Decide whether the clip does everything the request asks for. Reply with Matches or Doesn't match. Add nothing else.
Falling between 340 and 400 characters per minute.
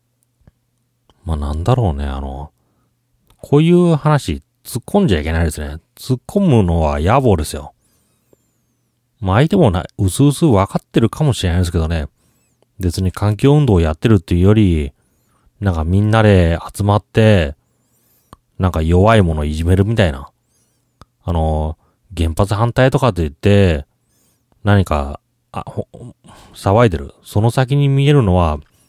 Doesn't match